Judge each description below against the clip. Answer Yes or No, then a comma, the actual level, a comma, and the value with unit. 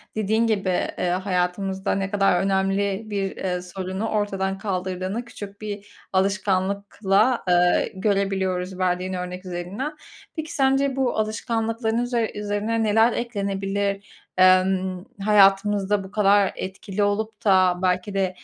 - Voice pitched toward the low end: No, high, 195 Hz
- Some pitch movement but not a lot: No, narrow, 2.3 semitones